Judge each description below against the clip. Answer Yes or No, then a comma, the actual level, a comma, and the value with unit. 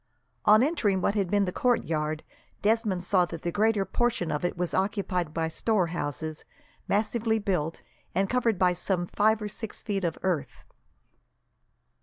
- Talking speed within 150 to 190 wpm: Yes, average, 155 wpm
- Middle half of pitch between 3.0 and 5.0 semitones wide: Yes, average, 3.8 semitones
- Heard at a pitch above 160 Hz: Yes, high, 190 Hz